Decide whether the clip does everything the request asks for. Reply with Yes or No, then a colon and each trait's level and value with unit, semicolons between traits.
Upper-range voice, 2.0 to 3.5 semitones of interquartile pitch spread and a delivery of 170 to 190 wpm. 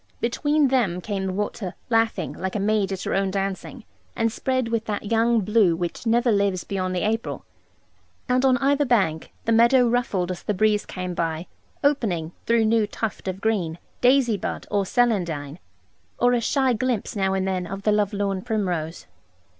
No: high, 210 Hz; average, 3.9 semitones; average, 180 wpm